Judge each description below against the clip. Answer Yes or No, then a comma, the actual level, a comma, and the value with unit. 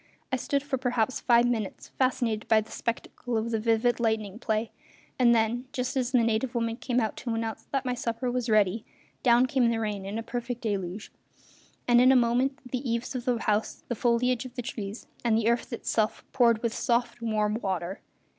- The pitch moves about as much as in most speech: No, narrow, 2.1 semitones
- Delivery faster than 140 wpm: Yes, average, 200 wpm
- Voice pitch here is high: Yes, high, 235 Hz